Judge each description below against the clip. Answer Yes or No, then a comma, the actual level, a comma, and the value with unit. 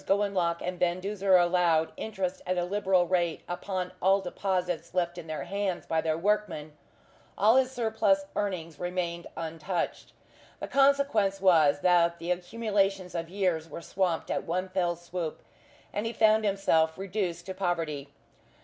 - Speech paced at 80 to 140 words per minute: No, average, 150 wpm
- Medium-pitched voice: Yes, medium, 180 Hz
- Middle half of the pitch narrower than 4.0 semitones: Yes, narrow, 2.6 semitones